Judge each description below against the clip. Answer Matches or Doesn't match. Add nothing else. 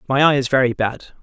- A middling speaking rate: Doesn't match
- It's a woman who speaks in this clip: Doesn't match